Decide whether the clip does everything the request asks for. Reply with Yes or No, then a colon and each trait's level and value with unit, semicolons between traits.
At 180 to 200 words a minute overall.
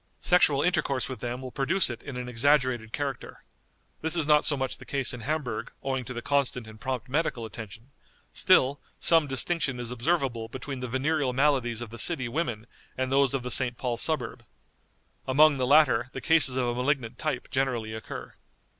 Yes: average, 190 wpm